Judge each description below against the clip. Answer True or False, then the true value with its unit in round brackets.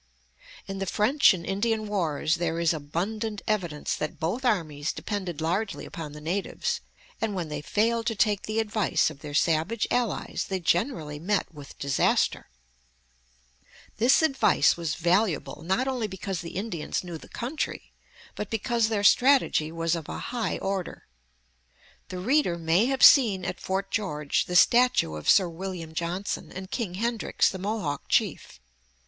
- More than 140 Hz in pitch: True (190 Hz)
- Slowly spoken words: False (160 wpm)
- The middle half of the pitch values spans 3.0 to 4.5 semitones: False (5.1 semitones)